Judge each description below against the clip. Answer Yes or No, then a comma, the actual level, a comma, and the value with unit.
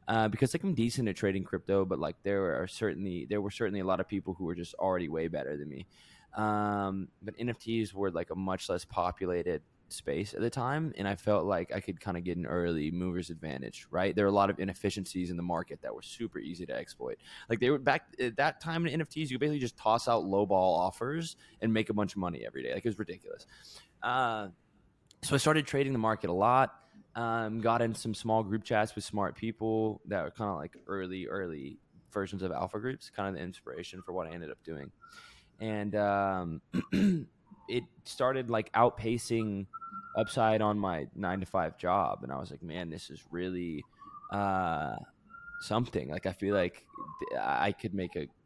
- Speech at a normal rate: No, fast, 210 wpm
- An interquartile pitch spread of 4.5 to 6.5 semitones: No, average, 3.9 semitones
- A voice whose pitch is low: Yes, low, 105 Hz